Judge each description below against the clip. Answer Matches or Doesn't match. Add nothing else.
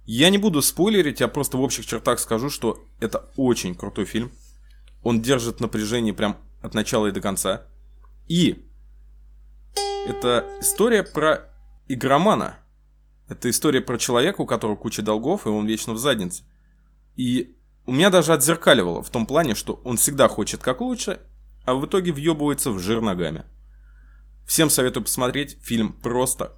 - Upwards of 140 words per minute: Matches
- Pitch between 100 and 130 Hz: Matches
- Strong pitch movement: Matches